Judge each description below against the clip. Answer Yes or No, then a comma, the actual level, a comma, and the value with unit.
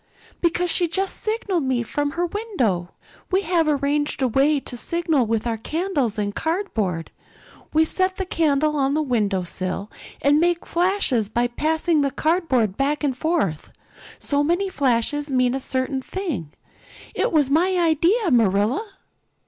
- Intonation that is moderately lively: No, wide, 6.1 semitones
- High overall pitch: Yes, very high, 290 Hz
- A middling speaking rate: Yes, average, 155 wpm